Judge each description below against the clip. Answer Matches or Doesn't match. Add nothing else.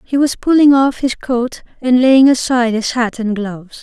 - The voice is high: Matches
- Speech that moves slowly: Doesn't match